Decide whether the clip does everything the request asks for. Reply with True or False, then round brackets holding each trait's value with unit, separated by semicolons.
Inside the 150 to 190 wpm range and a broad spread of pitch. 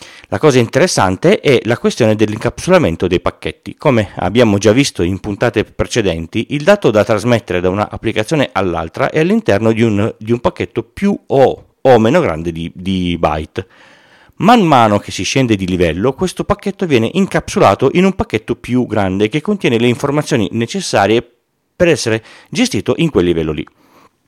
True (165 wpm; 7.7 semitones)